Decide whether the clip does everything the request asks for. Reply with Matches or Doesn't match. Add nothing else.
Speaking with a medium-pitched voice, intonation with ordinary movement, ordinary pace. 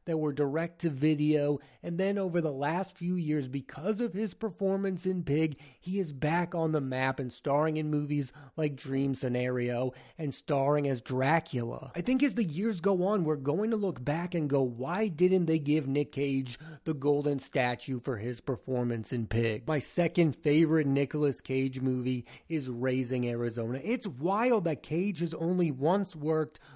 Matches